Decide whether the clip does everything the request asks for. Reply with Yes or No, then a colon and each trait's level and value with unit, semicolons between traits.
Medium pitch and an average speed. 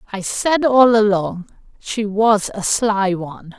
No: high, 210 Hz; average, 150 wpm